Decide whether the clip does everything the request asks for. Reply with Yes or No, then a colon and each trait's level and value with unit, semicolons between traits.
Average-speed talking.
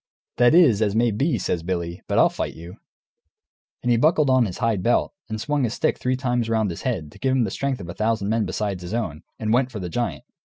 No: fast, 250 wpm